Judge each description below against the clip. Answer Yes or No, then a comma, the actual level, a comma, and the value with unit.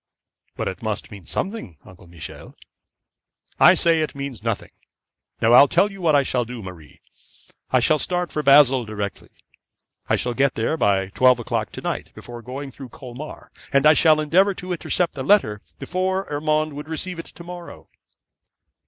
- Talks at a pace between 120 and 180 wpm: Yes, average, 175 wpm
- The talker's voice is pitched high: No, medium, 140 Hz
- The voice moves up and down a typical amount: No, wide, 6.0 semitones